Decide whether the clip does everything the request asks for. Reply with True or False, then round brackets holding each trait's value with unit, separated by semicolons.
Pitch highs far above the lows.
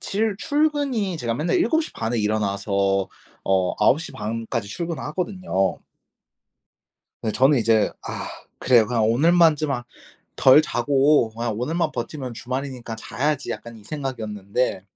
True (6.1 semitones)